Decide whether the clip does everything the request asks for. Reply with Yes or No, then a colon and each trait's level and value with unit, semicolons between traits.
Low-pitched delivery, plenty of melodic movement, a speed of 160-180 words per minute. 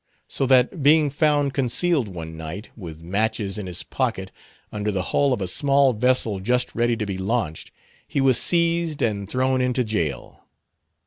Yes: low, 120 Hz; wide, 5.7 semitones; average, 170 wpm